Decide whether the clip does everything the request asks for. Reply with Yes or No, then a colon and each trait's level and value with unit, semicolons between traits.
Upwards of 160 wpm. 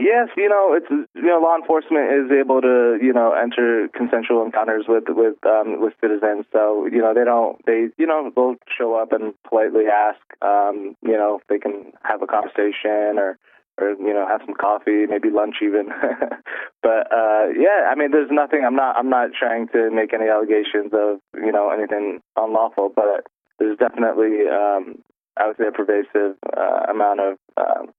Yes: average, 190 wpm